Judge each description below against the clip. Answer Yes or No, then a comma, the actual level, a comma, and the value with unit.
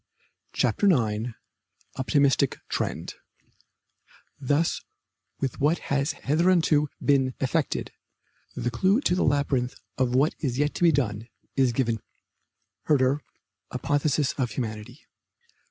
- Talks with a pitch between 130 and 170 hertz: Yes, medium, 140 Hz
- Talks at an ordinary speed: No, slow, 115 wpm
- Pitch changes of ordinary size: Yes, average, 3.2 semitones